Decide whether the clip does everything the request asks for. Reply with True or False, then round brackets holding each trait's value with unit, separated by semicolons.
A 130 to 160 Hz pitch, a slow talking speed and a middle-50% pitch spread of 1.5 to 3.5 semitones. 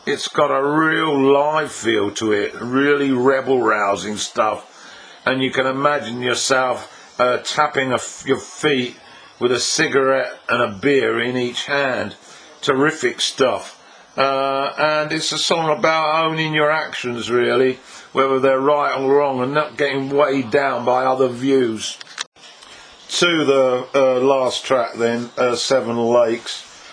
False (135 Hz; 145 wpm; 2.8 semitones)